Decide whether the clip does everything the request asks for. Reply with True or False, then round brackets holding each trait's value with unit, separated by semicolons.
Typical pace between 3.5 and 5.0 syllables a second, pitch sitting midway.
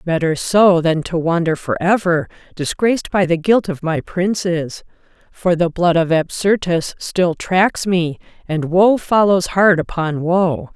True (4.0 syllables/s; 175 Hz)